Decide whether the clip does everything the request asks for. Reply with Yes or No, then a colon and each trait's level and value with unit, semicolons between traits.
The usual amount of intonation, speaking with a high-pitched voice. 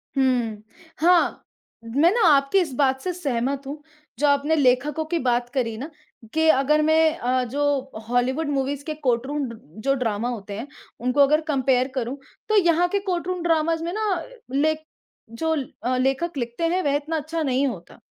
Yes: average, 4.1 semitones; very high, 280 Hz